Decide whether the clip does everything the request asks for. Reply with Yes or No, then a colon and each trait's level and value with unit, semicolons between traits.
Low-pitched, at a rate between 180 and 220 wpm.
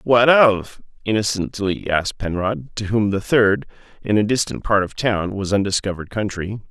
No: low, 105 Hz; average, 145 wpm